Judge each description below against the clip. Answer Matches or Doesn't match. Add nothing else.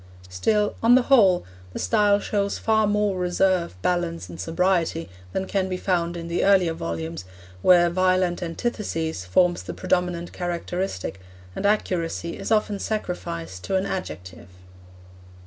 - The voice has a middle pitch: Matches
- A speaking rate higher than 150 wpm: Doesn't match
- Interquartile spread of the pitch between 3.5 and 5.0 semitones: Doesn't match